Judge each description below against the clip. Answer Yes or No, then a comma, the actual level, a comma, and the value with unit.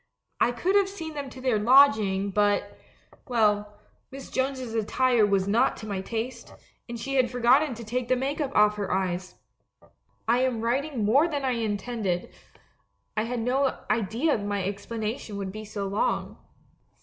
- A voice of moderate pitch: No, high, 230 Hz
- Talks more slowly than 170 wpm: No, average, 175 wpm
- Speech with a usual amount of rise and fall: Yes, average, 4.0 semitones